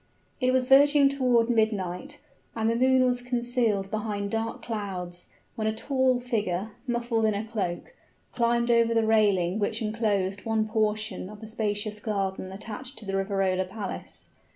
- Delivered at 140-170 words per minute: Yes, average, 155 wpm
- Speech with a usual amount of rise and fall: Yes, average, 3.0 semitones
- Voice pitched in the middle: No, high, 220 Hz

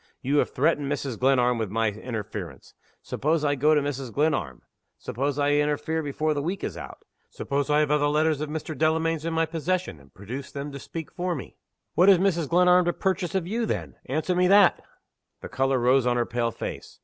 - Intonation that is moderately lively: Yes, average, 4.0 semitones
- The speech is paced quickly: Yes, fast, 210 wpm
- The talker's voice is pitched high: No, medium, 145 Hz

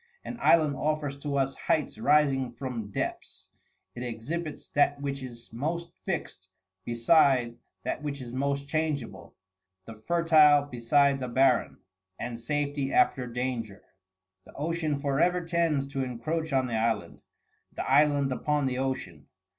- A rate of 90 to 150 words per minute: Yes, average, 140 wpm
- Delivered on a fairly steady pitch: No, average, 3.5 semitones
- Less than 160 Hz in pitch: Yes, medium, 140 Hz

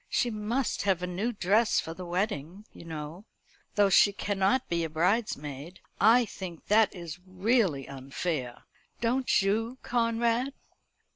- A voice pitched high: Yes, high, 195 Hz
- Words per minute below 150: Yes, average, 140 wpm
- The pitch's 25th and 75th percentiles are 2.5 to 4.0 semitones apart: No, average, 5.1 semitones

